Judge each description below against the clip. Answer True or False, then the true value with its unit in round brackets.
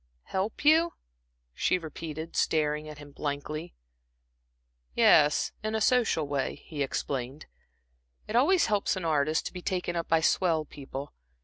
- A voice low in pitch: False (160 Hz)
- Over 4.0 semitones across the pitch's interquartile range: True (4.4 semitones)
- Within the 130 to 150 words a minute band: True (140 wpm)